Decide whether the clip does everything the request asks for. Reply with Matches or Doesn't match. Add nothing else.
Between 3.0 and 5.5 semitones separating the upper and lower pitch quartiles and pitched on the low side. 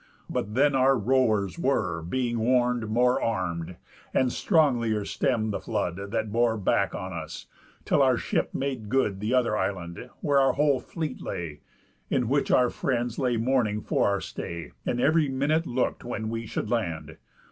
Matches